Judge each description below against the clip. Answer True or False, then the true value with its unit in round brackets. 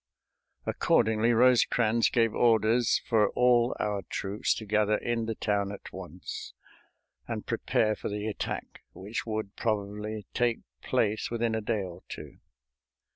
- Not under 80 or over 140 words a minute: True (135 wpm)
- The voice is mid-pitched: False (110 Hz)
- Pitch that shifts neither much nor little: False (1.9 semitones)